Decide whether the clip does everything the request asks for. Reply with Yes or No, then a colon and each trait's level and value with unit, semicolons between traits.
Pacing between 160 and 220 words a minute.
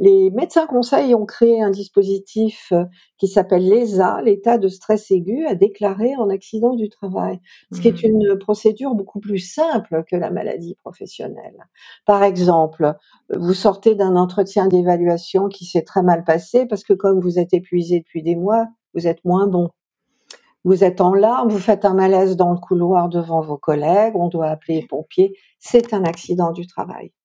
Yes: average, 180 wpm